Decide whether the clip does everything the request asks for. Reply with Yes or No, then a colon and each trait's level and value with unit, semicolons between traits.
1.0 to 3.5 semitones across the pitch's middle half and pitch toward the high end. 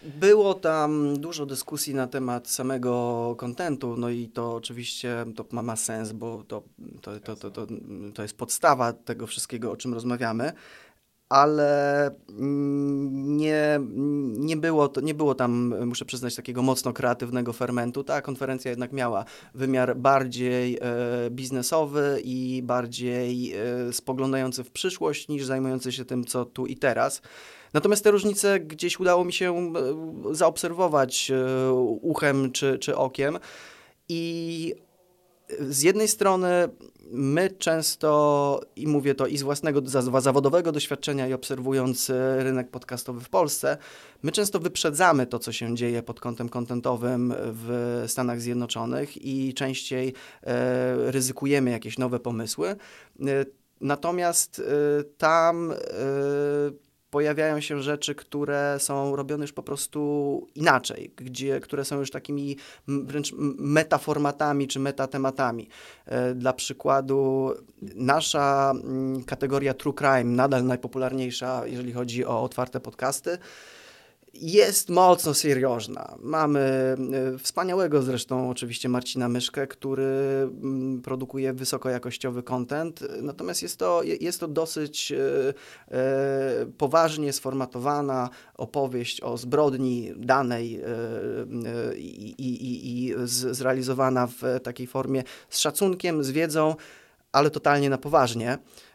No: average, 2.8 semitones; low, 135 Hz